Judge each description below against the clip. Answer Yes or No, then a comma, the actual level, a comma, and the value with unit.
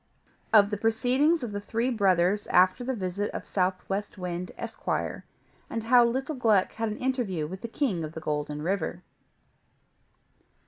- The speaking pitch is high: Yes, high, 205 Hz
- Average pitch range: Yes, average, 4.5 semitones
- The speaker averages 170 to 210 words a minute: No, average, 155 wpm